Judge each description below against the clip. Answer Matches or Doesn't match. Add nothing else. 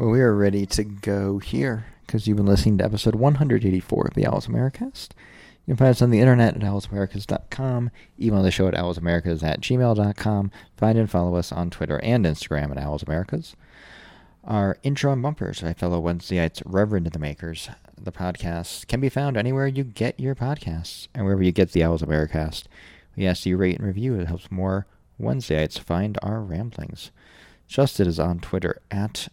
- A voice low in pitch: Matches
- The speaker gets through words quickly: Doesn't match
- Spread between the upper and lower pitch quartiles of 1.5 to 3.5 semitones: Doesn't match